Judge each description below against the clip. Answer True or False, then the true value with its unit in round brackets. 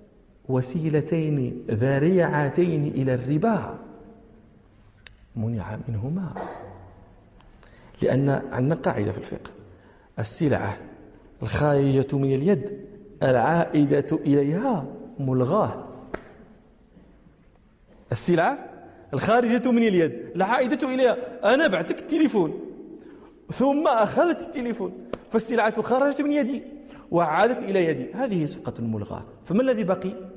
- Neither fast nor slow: True (85 wpm)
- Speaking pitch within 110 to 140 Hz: False (170 Hz)